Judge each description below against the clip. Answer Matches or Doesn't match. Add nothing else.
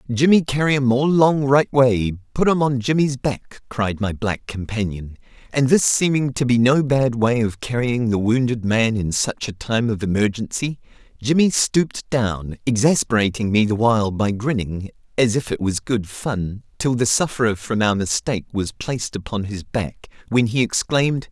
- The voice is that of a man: Matches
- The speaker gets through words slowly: Doesn't match